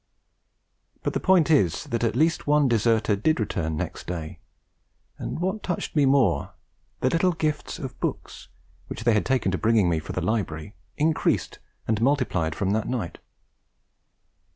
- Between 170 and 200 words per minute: No, average, 160 wpm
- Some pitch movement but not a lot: No, wide, 7.3 semitones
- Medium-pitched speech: No, low, 115 Hz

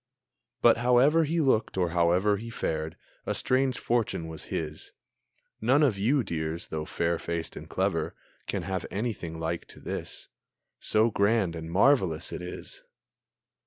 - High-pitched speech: No, very low, 95 Hz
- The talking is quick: No, average, 155 wpm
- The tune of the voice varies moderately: No, wide, 6.4 semitones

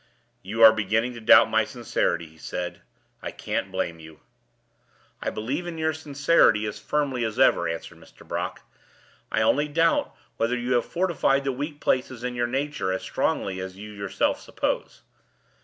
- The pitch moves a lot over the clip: Yes, wide, 6.4 semitones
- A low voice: Yes, low, 120 Hz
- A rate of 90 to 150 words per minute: No, average, 170 wpm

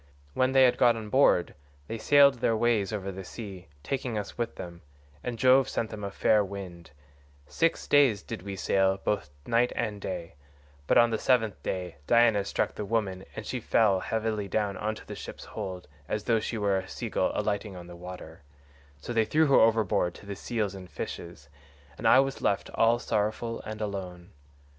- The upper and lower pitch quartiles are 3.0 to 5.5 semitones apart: Yes, average, 3.5 semitones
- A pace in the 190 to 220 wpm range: Yes, average, 195 wpm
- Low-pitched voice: Yes, low, 105 Hz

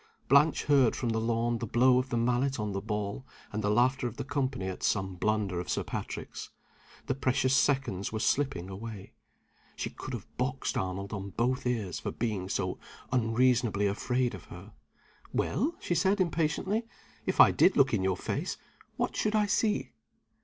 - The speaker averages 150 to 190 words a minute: Yes, average, 180 wpm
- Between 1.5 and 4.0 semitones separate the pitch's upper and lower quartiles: No, average, 4.8 semitones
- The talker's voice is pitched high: No, low, 120 Hz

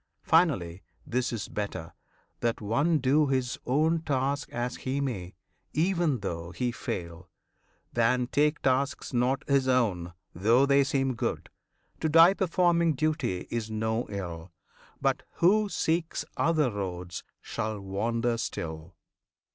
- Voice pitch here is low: Yes, low, 125 Hz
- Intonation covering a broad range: Yes, wide, 6.4 semitones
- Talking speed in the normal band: No, slow, 130 wpm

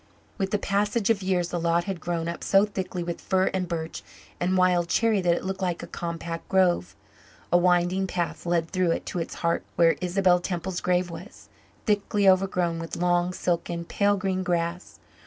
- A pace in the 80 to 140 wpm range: No, average, 190 wpm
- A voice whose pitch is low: No, medium, 180 Hz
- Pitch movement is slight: Yes, narrow, 1.9 semitones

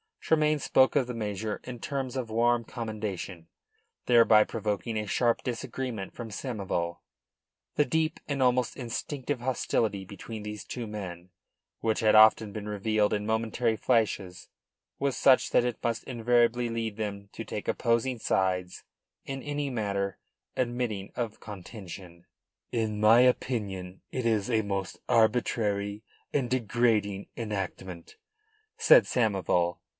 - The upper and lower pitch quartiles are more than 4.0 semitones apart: No, average, 3.3 semitones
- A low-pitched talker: Yes, low, 110 Hz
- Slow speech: Yes, slow, 130 wpm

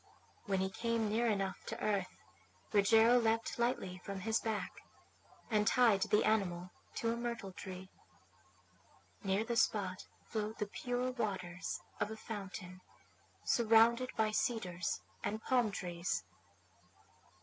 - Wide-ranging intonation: No, average, 3.2 semitones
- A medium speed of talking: No, slow, 125 wpm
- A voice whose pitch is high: Yes, high, 215 Hz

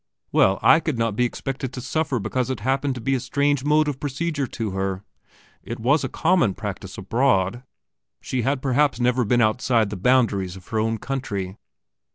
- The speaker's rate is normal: Yes, average, 190 wpm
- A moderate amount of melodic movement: Yes, average, 4.1 semitones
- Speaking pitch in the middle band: No, low, 125 Hz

